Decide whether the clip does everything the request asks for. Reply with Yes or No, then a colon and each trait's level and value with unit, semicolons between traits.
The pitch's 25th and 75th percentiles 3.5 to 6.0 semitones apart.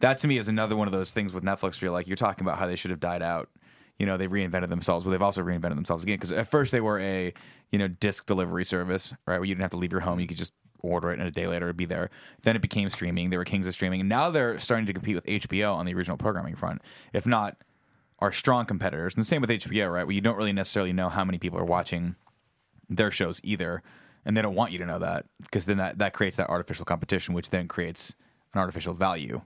No: average, 2.7 semitones